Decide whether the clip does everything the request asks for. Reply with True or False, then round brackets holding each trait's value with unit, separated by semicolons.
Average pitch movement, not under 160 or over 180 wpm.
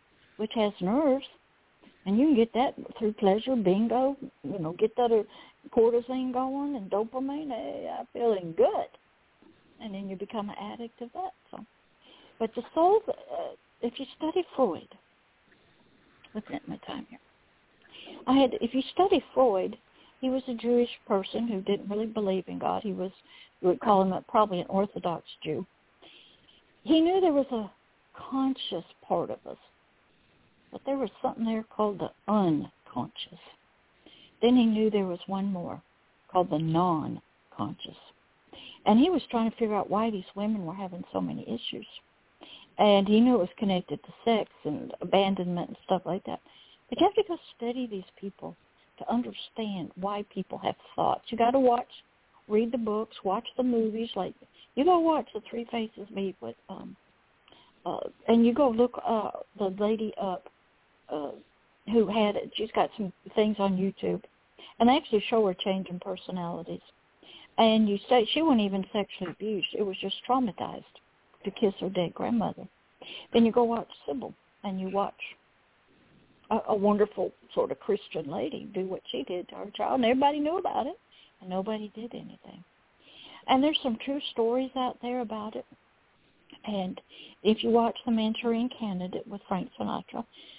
True (4.2 semitones; 170 wpm)